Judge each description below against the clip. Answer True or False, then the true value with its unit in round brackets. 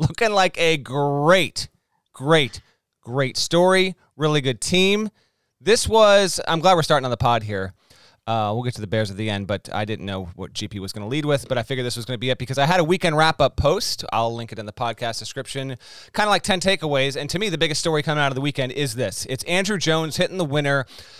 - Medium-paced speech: False (250 wpm)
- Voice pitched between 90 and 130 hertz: False (140 Hz)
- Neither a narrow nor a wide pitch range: False (6.4 semitones)